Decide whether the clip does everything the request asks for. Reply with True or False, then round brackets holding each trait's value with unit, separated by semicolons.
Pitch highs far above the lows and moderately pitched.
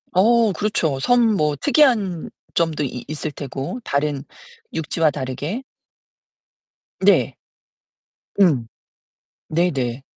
True (6.3 semitones; 155 Hz)